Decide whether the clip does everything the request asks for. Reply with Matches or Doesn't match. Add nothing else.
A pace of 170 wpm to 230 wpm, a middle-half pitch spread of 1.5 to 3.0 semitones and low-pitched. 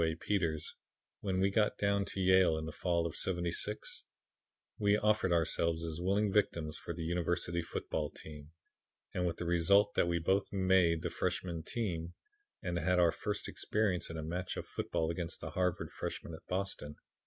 Matches